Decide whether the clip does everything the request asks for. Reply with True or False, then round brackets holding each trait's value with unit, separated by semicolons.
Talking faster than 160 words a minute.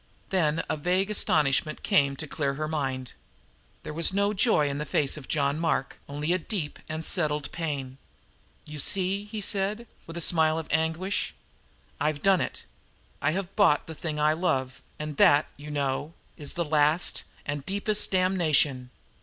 True (170 wpm)